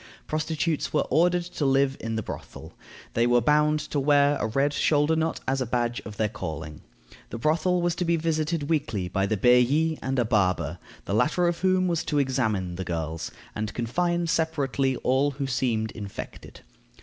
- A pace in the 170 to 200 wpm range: Yes, average, 185 wpm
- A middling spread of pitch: No, wide, 6.1 semitones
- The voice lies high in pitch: No, low, 135 Hz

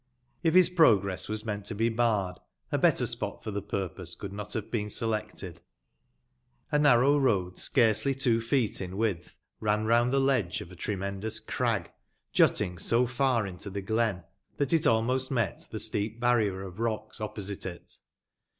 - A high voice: No, low, 110 Hz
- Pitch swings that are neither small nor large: Yes, average, 3.6 semitones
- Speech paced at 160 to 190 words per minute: Yes, average, 170 wpm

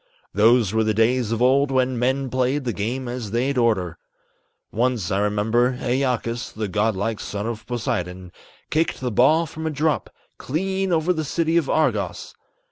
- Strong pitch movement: No, average, 4.0 semitones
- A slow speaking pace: No, average, 170 wpm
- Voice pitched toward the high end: No, low, 125 Hz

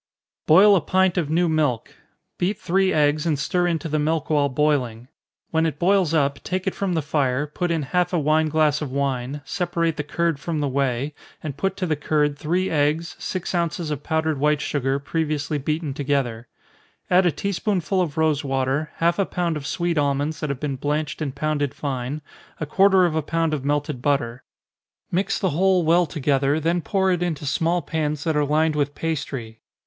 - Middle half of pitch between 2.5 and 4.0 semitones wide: Yes, average, 3.0 semitones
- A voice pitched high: No, medium, 155 Hz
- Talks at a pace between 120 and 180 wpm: No, average, 200 wpm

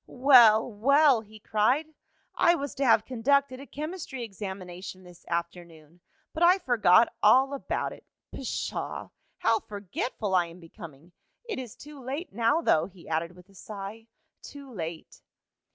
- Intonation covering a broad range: Yes, wide, 7.3 semitones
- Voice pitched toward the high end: Yes, high, 220 Hz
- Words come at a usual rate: Yes, average, 150 wpm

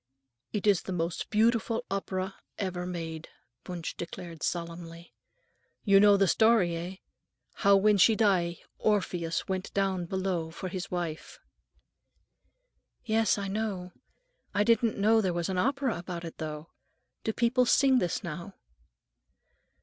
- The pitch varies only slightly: No, average, 3.7 semitones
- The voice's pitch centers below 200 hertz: Yes, high, 190 Hz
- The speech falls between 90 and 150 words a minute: Yes, average, 140 wpm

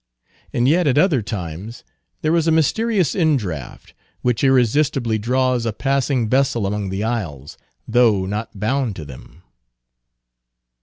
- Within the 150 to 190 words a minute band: No, slow, 135 wpm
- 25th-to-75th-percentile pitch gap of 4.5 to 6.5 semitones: Yes, average, 5.1 semitones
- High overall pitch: No, low, 120 Hz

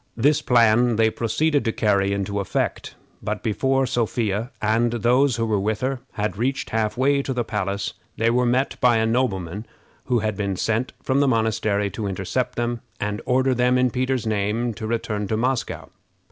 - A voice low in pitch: Yes, low, 115 Hz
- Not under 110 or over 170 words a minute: No, average, 185 wpm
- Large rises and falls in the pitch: No, average, 3.2 semitones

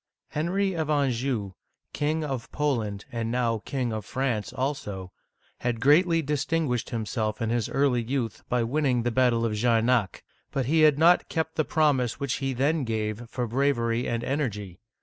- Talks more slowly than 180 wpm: Yes, average, 170 wpm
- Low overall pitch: Yes, low, 125 Hz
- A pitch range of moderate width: Yes, average, 4.2 semitones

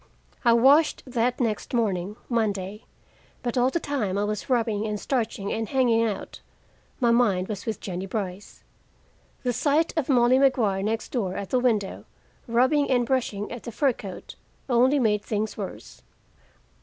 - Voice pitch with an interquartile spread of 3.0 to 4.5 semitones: Yes, average, 3.5 semitones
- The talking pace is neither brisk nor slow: Yes, average, 160 wpm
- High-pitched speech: Yes, high, 230 Hz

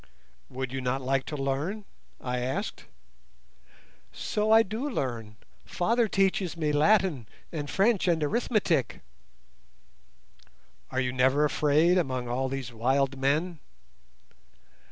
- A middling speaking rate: No, slow, 120 wpm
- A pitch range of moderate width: No, wide, 5.9 semitones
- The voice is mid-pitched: Yes, medium, 145 Hz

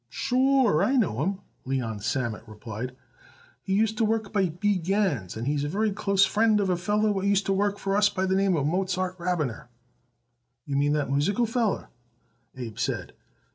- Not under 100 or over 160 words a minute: No, average, 180 wpm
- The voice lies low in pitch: No, high, 190 Hz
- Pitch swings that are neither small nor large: No, wide, 6.6 semitones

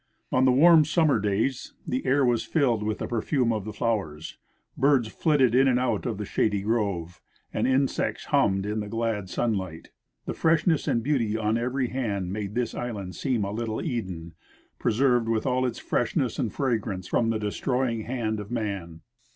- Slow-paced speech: No, average, 180 wpm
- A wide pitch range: No, average, 3.7 semitones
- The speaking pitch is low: Yes, low, 115 Hz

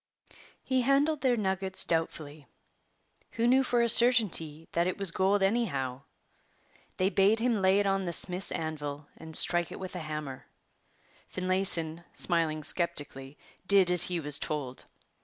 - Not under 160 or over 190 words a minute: No, average, 150 wpm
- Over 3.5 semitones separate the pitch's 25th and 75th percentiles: Yes, average, 4.5 semitones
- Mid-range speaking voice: Yes, medium, 180 Hz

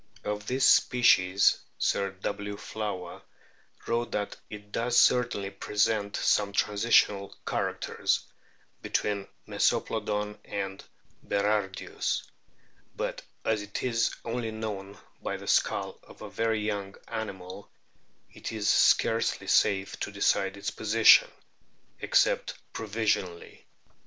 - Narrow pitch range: Yes, narrow, 1.9 semitones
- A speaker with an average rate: No, slow, 105 wpm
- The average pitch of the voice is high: No, low, 105 Hz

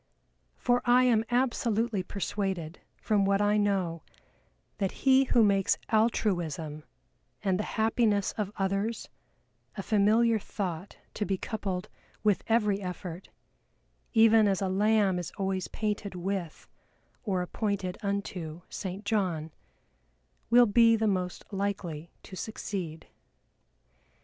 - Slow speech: Yes, slow, 120 wpm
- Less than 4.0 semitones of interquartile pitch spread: Yes, average, 3.0 semitones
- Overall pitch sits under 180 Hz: No, high, 200 Hz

